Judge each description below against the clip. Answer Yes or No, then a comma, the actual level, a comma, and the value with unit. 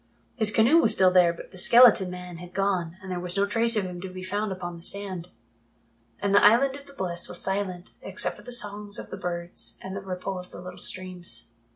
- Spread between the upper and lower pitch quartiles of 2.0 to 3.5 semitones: Yes, narrow, 2.5 semitones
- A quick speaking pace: Yes, fast, 240 wpm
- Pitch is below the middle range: No, medium, 185 Hz